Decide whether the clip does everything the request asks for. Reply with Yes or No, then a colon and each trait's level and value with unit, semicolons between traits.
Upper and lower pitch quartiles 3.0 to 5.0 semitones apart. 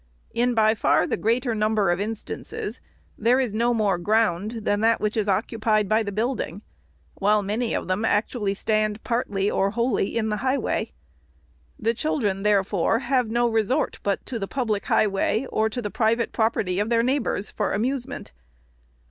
No: narrow, 2.4 semitones